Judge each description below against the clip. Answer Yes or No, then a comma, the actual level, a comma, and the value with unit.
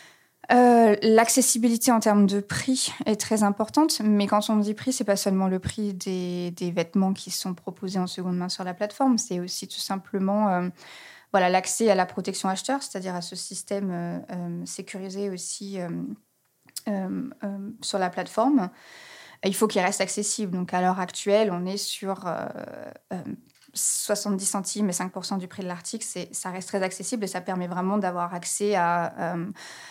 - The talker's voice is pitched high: Yes, high, 195 Hz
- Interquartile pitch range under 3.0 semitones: Yes, narrow, 2.4 semitones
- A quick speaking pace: No, average, 185 wpm